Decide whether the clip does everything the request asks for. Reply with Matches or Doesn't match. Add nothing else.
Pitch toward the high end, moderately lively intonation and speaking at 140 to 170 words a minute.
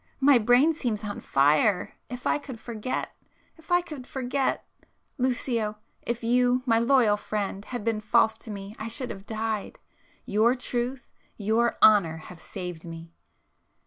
Matches